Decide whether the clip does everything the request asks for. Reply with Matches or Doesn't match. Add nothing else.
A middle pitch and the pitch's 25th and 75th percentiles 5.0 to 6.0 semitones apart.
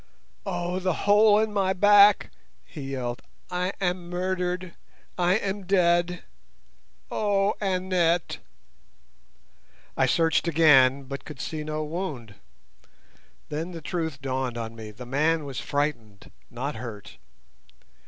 Matches